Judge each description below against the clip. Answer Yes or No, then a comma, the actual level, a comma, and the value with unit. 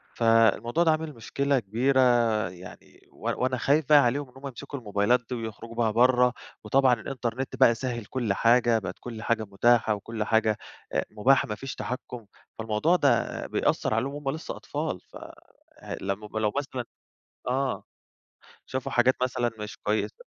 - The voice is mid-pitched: No, low, 120 Hz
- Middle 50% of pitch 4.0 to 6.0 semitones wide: No, average, 3.2 semitones